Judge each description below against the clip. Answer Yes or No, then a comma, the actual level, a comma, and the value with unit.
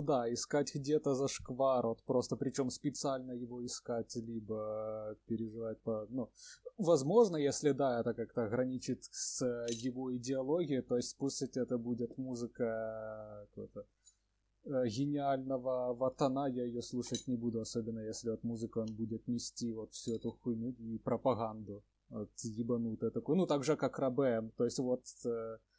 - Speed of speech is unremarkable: Yes, average, 145 wpm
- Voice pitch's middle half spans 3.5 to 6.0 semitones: No, average, 2.9 semitones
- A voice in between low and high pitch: No, low, 120 Hz